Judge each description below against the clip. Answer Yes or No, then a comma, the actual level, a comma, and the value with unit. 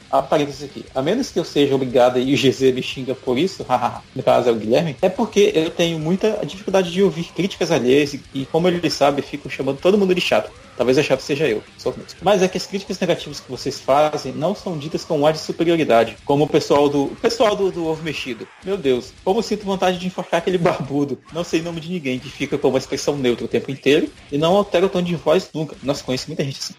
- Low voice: No, medium, 155 Hz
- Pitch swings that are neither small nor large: Yes, average, 5.0 semitones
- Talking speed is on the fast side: Yes, fast, 250 wpm